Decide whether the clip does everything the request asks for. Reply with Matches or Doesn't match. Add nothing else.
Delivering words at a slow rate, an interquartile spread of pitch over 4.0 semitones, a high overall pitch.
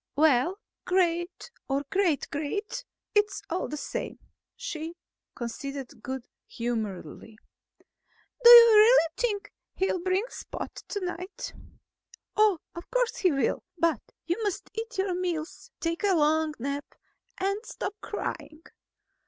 Matches